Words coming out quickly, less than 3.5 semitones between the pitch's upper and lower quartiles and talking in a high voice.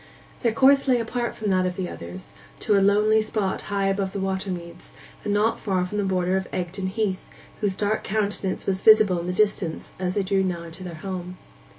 Yes: fast, 215 wpm; narrow, 2.4 semitones; high, 195 Hz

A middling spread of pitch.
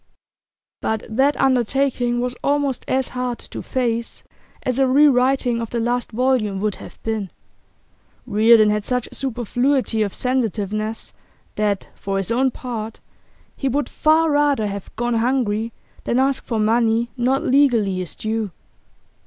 Yes: average, 3.3 semitones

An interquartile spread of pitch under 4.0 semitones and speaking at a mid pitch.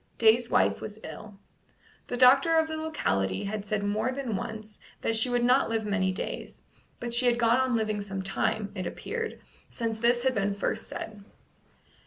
No: average, 3.4 semitones; high, 225 Hz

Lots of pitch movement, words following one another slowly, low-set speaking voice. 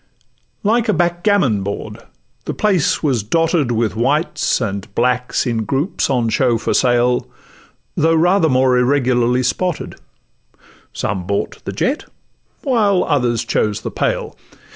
Yes: wide, 6.1 semitones; slow, 130 wpm; low, 130 Hz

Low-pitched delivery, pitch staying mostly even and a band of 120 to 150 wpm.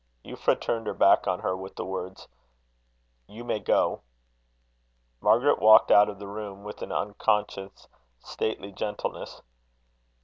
Yes: low, 105 Hz; narrow, 1.8 semitones; slow, 135 wpm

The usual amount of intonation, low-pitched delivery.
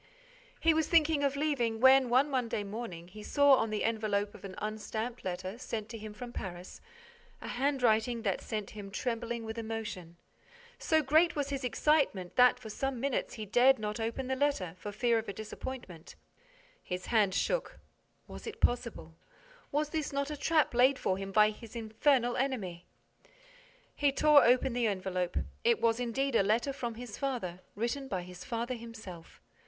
No: average, 4.3 semitones; high, 235 Hz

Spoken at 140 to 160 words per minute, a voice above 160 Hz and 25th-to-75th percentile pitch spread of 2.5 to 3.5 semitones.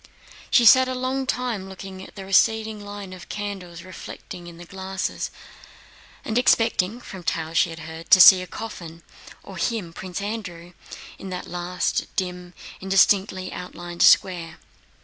Yes: average, 150 wpm; high, 190 Hz; average, 2.9 semitones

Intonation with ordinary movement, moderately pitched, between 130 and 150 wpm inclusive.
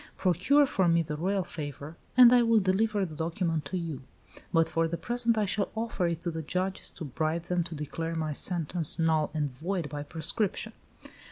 No: average, 3.5 semitones; medium, 170 Hz; average, 195 wpm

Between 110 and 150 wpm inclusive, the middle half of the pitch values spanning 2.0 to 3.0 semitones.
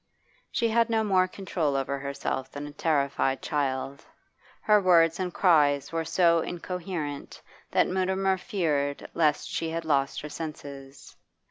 No: average, 140 wpm; average, 4.6 semitones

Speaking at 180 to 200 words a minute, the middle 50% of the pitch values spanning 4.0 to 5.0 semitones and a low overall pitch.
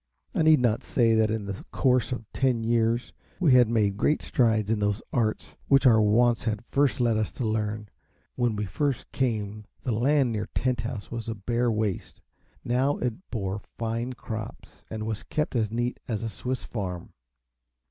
No: average, 185 wpm; narrow, 2.5 semitones; low, 115 Hz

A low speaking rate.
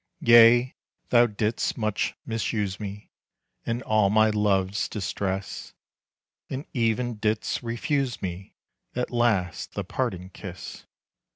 Yes: slow, 110 wpm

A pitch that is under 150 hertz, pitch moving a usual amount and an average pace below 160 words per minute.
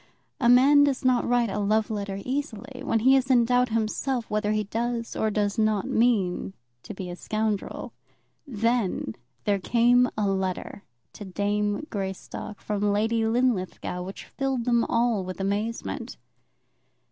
No: high, 220 Hz; average, 3.3 semitones; average, 150 wpm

